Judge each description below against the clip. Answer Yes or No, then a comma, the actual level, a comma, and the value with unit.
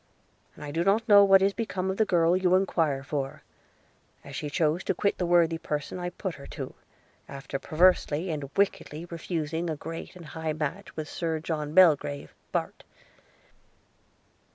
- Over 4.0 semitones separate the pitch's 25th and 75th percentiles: No, average, 3.6 semitones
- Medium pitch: Yes, medium, 165 Hz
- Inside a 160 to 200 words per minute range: Yes, average, 165 wpm